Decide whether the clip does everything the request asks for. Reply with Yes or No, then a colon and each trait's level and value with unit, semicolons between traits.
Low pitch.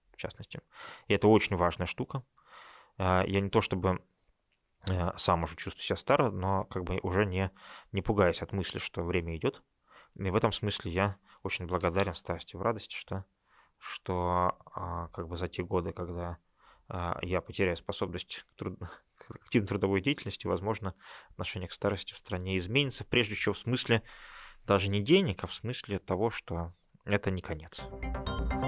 Yes: very low, 95 Hz